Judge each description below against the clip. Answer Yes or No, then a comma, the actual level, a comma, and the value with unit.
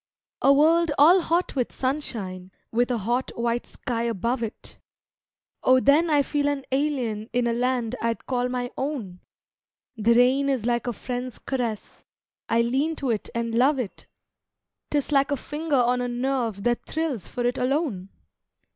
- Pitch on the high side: Yes, very high, 250 Hz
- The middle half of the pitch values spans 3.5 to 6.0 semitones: No, average, 3.1 semitones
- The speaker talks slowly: No, average, 165 wpm